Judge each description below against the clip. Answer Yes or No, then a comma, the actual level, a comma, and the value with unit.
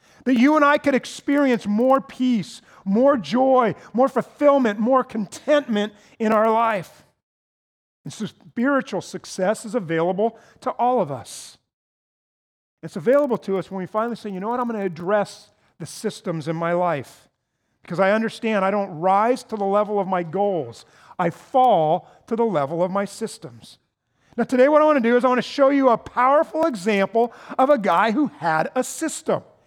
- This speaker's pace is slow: No, average, 180 wpm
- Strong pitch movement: No, average, 4.9 semitones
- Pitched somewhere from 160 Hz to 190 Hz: No, high, 220 Hz